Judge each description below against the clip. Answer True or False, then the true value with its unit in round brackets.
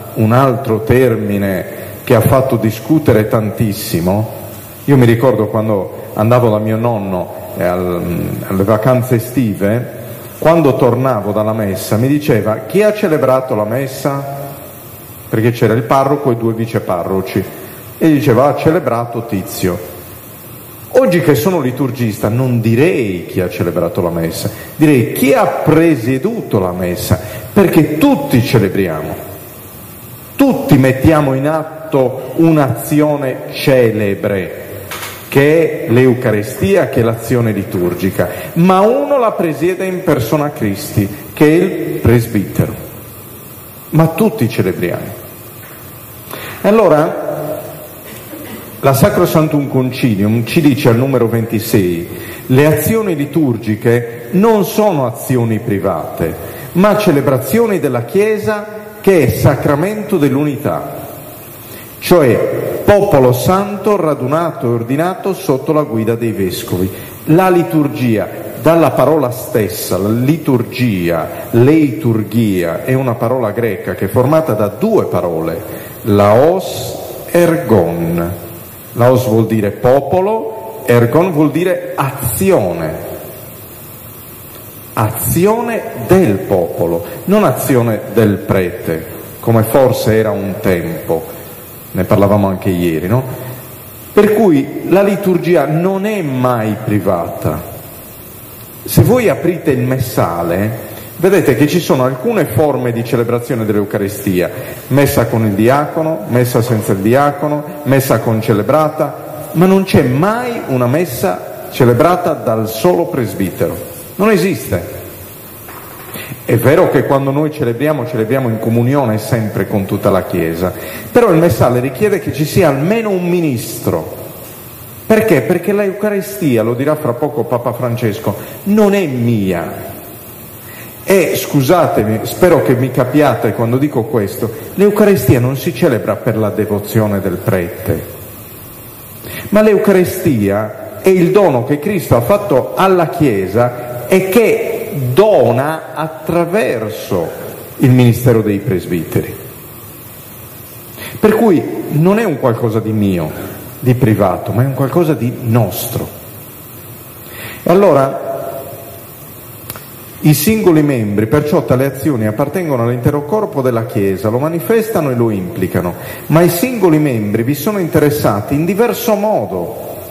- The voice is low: True (125 Hz)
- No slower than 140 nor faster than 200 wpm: False (120 wpm)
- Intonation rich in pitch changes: True (6.1 semitones)